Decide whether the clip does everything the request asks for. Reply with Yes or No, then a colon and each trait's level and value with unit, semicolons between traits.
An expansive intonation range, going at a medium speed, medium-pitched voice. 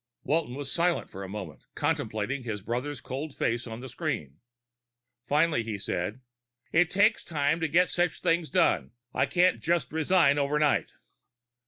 Yes: wide, 6.0 semitones; average, 155 wpm; medium, 145 Hz